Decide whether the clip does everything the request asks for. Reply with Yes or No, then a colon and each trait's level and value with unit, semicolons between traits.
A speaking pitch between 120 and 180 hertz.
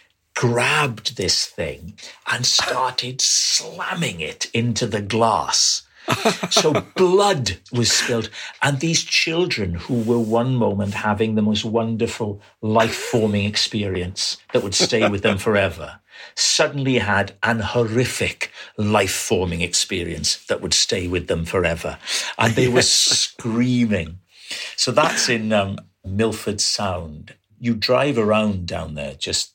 No: low, 110 Hz